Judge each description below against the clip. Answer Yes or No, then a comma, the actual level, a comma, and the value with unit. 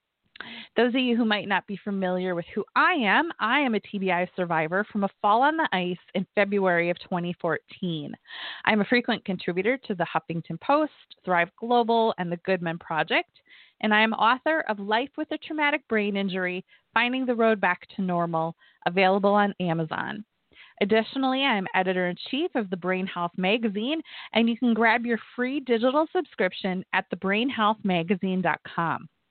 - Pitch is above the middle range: Yes, high, 205 Hz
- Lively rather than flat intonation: No, average, 4.6 semitones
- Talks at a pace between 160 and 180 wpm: Yes, average, 170 wpm